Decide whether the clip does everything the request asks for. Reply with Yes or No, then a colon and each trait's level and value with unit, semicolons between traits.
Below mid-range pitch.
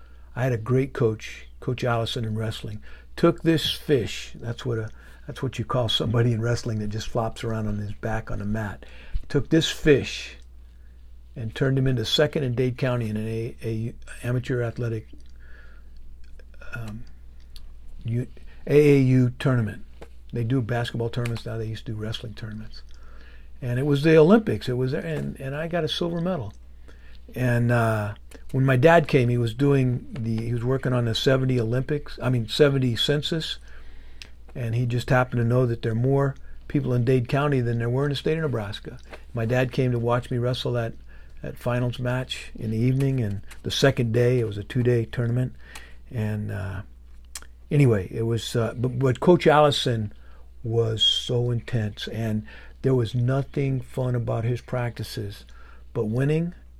Yes: low, 120 Hz